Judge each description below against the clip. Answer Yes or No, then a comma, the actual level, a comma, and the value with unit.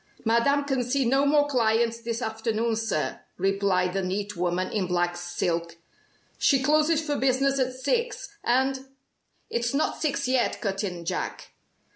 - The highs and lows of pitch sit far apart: Yes, wide, 5.8 semitones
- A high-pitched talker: Yes, high, 235 Hz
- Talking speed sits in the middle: Yes, average, 155 wpm